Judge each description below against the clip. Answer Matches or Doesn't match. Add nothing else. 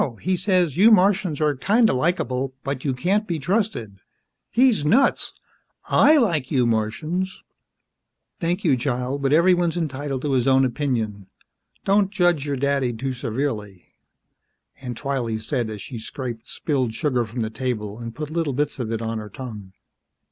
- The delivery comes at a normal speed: Matches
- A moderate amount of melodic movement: Doesn't match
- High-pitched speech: Doesn't match